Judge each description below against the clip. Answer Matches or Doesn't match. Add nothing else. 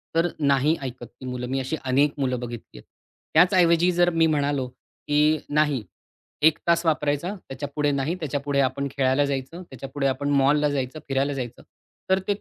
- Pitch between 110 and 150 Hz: Matches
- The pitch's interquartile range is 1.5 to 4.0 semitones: Matches